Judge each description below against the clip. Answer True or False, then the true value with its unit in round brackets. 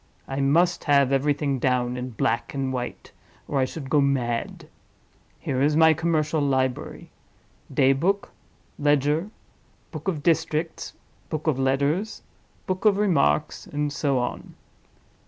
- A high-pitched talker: False (145 Hz)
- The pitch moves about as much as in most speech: True (3.2 semitones)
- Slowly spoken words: True (130 wpm)